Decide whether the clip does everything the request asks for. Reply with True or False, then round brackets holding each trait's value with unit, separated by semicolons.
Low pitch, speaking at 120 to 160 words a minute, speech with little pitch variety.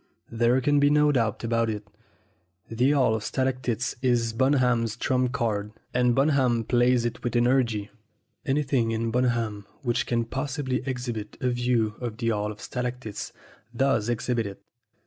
True (120 Hz; 155 wpm; 2.3 semitones)